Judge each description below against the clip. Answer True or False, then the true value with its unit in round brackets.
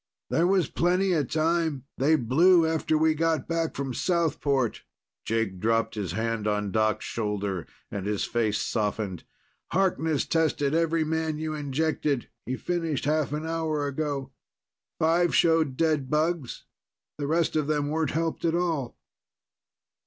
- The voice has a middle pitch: True (155 Hz)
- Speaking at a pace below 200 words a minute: True (145 wpm)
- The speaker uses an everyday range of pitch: True (4.8 semitones)